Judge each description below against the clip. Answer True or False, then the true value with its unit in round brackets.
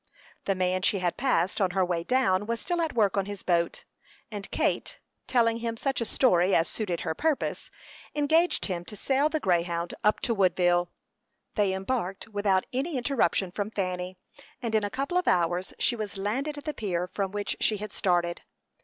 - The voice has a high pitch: True (205 Hz)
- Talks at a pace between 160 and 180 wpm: False (190 wpm)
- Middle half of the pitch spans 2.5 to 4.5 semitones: False (5.0 semitones)